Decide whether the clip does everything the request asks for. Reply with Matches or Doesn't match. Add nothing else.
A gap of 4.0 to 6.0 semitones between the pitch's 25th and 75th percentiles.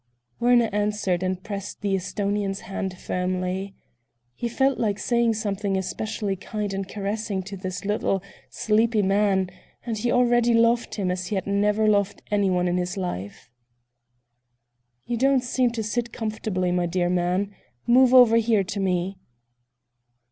Doesn't match